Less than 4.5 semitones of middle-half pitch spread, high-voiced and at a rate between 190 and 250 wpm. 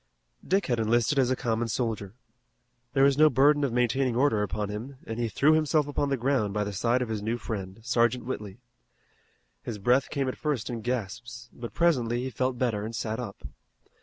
No: average, 3.3 semitones; low, 120 Hz; average, 200 wpm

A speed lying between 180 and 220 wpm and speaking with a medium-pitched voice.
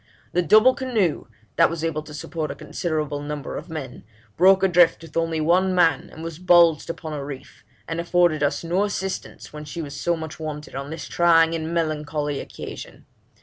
Yes: average, 190 wpm; medium, 165 Hz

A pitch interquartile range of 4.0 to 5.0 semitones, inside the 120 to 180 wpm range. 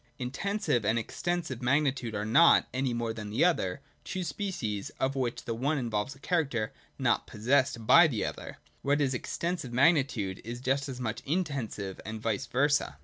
Yes: average, 4.4 semitones; average, 170 wpm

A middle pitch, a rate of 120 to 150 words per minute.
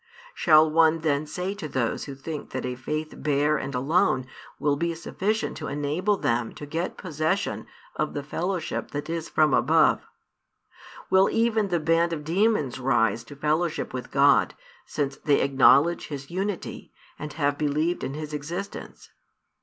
No: medium, 155 Hz; average, 160 wpm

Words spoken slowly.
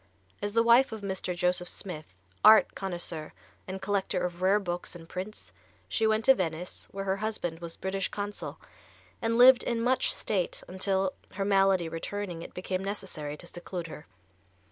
No: average, 165 wpm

